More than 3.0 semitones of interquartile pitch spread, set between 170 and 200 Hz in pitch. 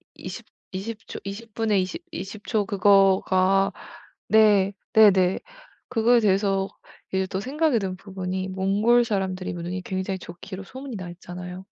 No: narrow, 2.5 semitones; high, 195 Hz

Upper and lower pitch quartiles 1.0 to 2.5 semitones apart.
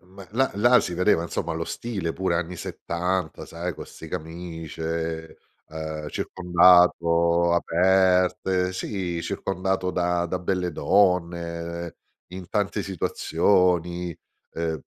Yes: narrow, 1.7 semitones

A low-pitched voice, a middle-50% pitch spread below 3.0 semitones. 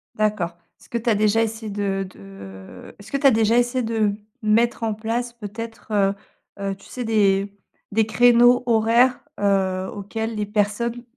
No: high, 220 Hz; narrow, 2.6 semitones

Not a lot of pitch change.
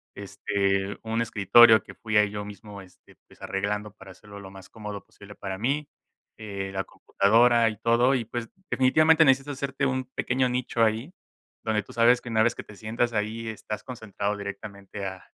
No: average, 3.2 semitones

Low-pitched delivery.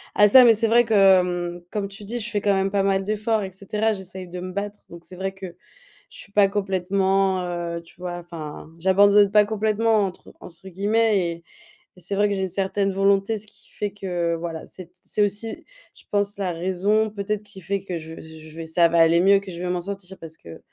No: high, 195 Hz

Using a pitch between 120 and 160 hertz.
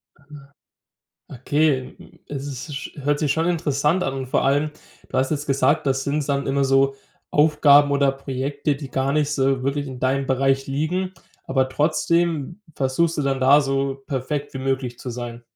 Yes: medium, 140 Hz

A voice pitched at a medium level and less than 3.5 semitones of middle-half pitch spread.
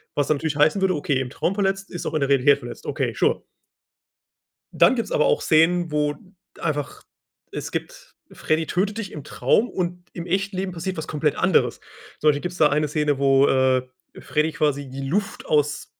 No: medium, 155 Hz; average, 4.1 semitones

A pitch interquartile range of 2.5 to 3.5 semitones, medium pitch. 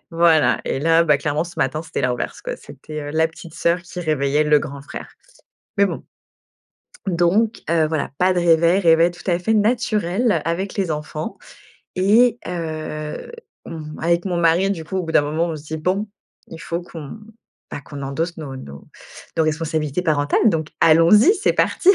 Yes: average, 2.8 semitones; medium, 165 Hz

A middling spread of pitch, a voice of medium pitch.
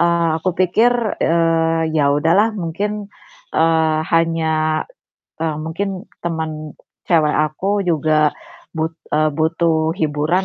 No: narrow, 1.8 semitones; medium, 165 Hz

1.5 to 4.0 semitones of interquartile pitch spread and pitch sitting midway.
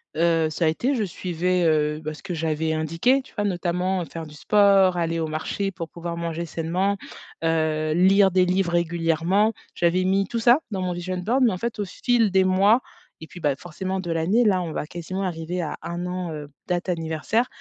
Yes: average, 2.9 semitones; medium, 175 Hz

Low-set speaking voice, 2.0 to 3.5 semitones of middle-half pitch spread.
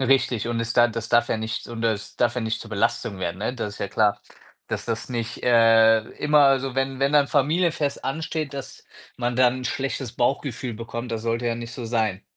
Yes: low, 120 Hz; average, 2.9 semitones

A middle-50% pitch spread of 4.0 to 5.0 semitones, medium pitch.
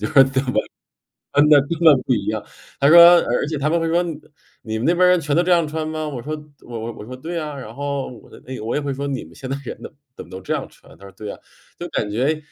Yes: average, 4.5 semitones; medium, 145 Hz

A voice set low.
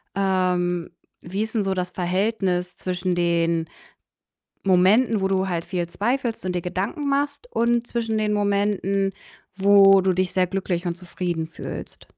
No: high, 190 Hz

